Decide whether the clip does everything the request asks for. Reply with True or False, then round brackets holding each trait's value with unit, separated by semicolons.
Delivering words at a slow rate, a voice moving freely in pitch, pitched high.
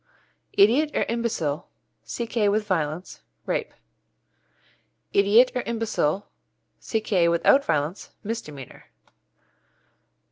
True (80 wpm; 5.7 semitones; 205 Hz)